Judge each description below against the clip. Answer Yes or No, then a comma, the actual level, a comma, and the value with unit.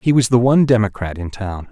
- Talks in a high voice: No, low, 110 Hz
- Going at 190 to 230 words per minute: No, fast, 245 wpm